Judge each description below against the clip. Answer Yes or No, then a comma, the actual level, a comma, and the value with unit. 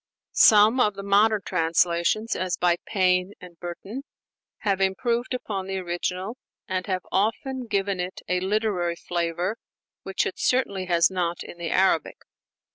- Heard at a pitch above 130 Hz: Yes, high, 190 Hz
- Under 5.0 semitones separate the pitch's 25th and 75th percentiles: Yes, average, 2.9 semitones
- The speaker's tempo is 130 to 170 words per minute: Yes, average, 145 wpm